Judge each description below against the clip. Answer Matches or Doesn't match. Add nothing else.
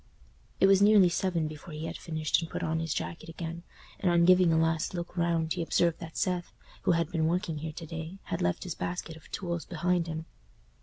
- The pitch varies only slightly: Matches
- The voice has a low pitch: Doesn't match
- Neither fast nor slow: Doesn't match